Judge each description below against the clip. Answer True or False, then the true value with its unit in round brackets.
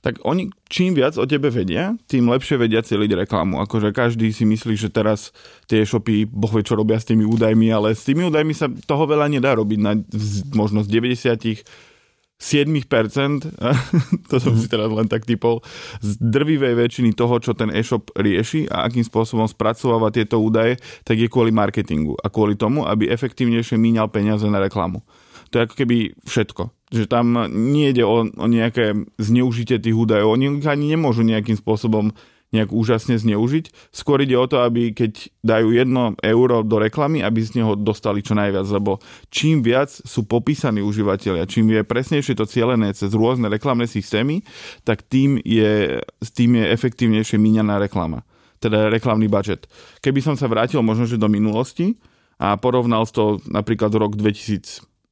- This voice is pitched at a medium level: False (115 Hz)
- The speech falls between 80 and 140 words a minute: False (165 wpm)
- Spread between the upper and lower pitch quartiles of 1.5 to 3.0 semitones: True (2.6 semitones)